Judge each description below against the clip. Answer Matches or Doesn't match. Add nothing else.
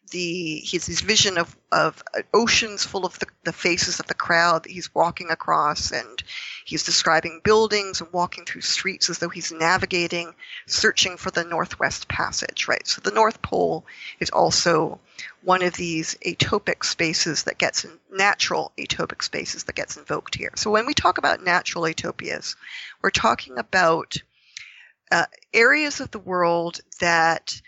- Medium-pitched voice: Matches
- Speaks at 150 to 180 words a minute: Matches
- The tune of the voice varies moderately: Doesn't match